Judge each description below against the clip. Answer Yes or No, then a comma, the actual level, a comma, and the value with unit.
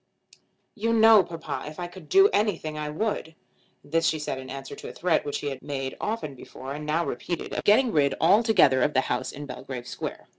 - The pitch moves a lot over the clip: Yes, wide, 6.5 semitones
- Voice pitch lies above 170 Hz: No, medium, 155 Hz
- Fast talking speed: Yes, fast, 215 wpm